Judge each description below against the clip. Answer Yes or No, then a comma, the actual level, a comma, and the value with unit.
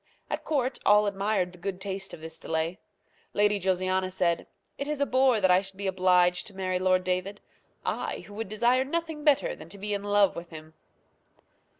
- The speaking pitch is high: Yes, high, 195 Hz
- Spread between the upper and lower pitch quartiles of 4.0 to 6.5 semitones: No, average, 2.8 semitones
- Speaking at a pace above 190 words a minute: Yes, average, 200 wpm